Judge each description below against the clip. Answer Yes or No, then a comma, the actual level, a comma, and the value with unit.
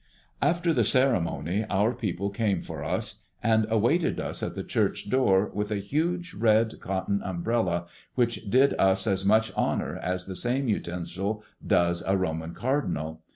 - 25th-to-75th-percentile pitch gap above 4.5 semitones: No, average, 4.2 semitones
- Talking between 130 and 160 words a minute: Yes, average, 155 wpm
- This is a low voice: Yes, low, 105 Hz